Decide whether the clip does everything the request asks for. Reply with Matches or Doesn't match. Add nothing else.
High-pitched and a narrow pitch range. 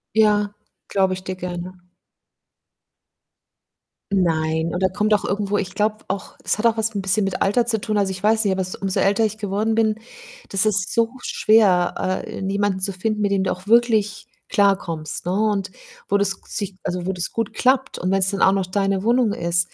Matches